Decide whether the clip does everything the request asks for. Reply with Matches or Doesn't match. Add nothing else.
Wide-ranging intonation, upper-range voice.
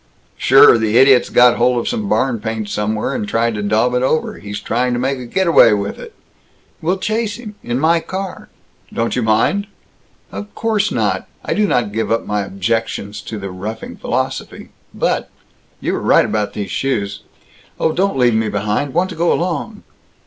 Doesn't match